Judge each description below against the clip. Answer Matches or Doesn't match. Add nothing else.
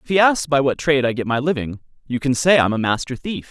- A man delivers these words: Matches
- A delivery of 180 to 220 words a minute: Doesn't match